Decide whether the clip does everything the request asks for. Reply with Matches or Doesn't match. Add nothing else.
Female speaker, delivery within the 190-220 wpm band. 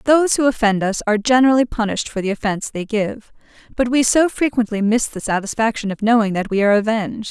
Matches